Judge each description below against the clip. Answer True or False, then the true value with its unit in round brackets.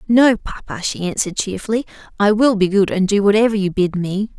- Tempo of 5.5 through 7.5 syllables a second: True (5.7 syllables/s)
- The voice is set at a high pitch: True (200 Hz)